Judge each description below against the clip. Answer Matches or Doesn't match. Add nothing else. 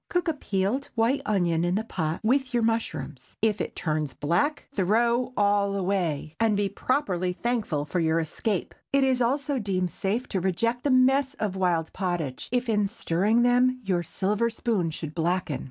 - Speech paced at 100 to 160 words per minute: Doesn't match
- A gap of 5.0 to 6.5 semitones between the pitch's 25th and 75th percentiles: Matches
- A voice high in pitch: Matches